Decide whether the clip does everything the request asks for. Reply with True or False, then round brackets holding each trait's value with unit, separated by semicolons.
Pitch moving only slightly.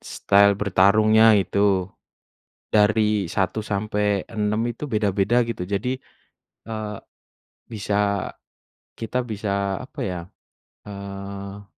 True (1.5 semitones)